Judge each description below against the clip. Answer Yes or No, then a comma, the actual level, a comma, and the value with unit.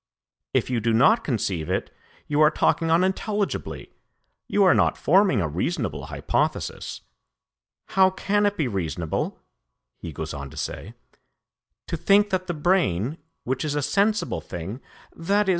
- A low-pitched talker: No, medium, 155 Hz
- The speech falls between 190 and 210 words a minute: No, average, 145 wpm